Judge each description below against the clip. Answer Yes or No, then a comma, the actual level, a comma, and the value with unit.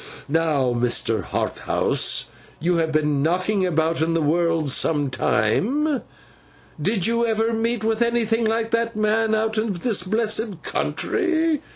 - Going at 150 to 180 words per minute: No, average, 140 wpm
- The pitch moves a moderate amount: No, wide, 6.1 semitones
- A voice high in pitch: Yes, high, 210 Hz